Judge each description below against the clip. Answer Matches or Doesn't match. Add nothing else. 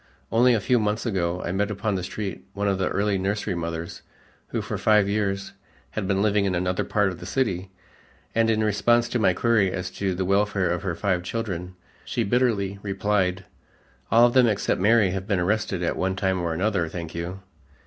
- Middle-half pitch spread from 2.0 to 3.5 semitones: Matches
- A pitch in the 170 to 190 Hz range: Doesn't match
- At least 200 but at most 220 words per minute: Matches